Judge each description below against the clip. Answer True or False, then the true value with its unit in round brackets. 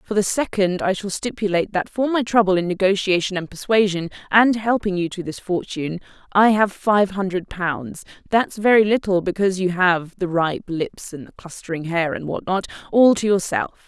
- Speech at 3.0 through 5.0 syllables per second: False (5.2 syllables/s)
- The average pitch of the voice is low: False (190 Hz)